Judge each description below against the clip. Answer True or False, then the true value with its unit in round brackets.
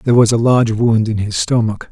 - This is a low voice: True (110 Hz)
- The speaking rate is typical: False (250 wpm)